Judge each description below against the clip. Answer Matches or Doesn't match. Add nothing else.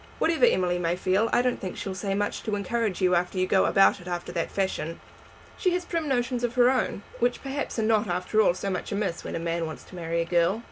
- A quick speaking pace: Matches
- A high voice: Matches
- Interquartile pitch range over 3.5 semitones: Matches